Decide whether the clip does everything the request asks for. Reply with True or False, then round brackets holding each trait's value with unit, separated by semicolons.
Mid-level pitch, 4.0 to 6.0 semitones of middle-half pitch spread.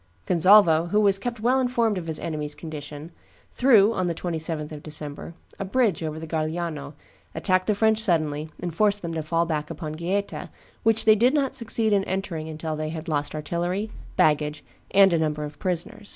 True (170 Hz; 4.7 semitones)